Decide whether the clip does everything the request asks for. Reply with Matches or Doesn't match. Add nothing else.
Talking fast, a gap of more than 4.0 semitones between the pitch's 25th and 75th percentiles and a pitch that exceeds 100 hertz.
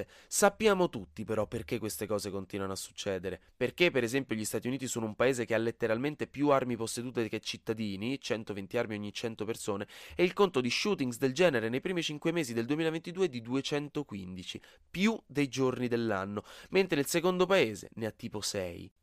Matches